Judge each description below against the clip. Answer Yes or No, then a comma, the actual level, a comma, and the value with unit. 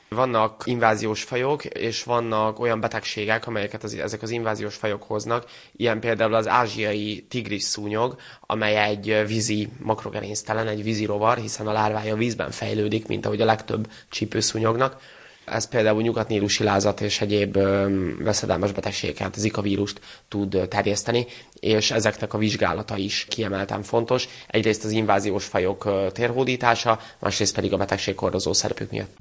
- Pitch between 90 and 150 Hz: Yes, low, 110 Hz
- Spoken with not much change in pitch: Yes, narrow, 1.5 semitones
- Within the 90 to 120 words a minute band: No, average, 140 wpm